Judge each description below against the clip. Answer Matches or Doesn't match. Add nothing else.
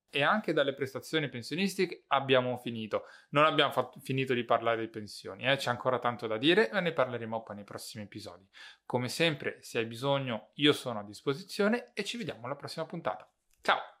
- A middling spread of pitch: Matches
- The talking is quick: Matches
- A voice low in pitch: Matches